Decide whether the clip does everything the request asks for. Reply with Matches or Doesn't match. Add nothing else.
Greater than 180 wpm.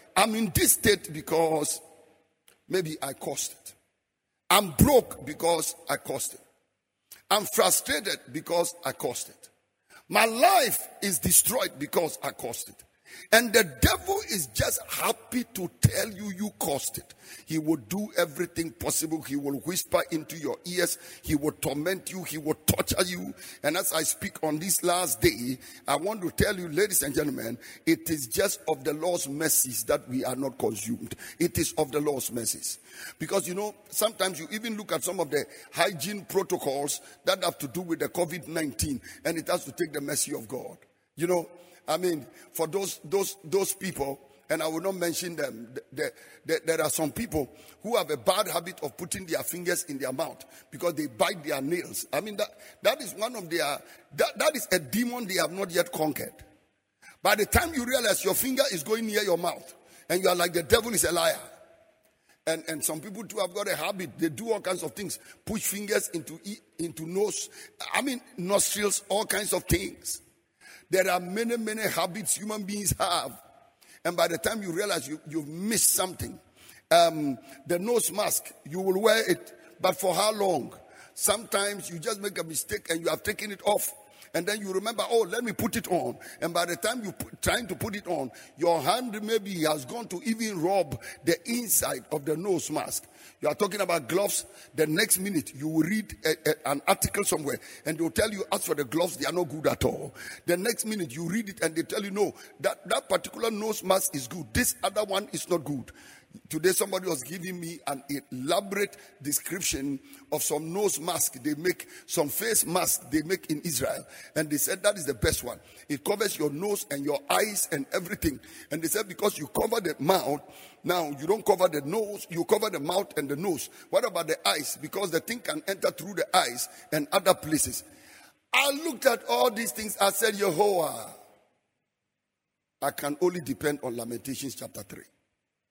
Matches